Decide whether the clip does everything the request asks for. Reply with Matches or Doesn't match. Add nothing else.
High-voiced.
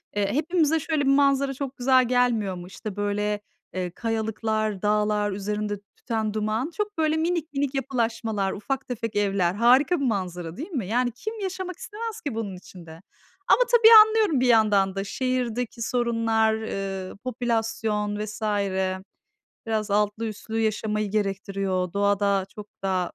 Matches